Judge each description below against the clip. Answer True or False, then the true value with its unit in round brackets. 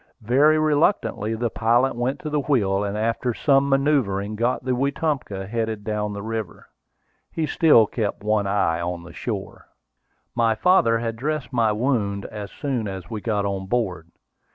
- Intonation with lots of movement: False (4.7 semitones)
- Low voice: True (115 Hz)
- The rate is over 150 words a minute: True (165 wpm)